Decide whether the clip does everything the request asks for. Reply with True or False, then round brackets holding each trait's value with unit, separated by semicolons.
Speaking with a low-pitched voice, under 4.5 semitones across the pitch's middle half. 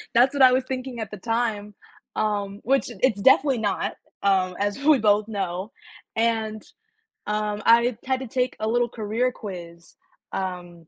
False (220 Hz; 3.7 semitones)